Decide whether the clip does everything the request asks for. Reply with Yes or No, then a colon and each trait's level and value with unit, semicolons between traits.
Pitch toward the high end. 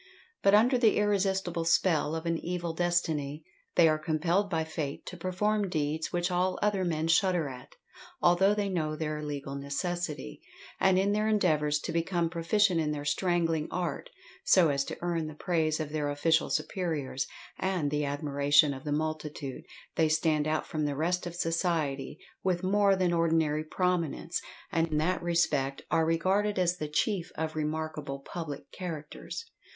No: medium, 165 Hz